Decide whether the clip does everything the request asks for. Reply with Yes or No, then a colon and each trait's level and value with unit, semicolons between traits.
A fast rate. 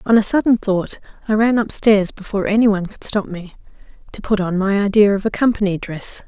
Yes: fast, 210 wpm